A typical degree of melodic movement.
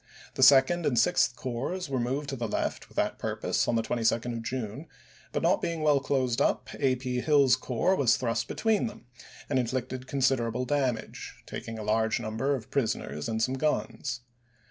Yes: average, 3.2 semitones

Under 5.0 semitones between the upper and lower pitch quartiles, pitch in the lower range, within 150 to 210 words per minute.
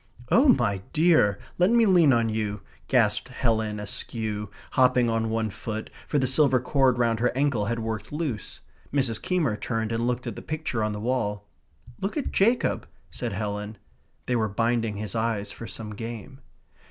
Yes: average, 3.6 semitones; low, 115 Hz; average, 175 wpm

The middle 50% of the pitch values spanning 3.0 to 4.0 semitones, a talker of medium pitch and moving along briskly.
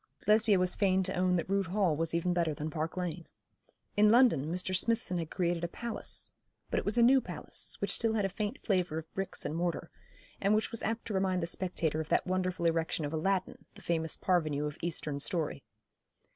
Yes: average, 3.3 semitones; medium, 180 Hz; fast, 215 wpm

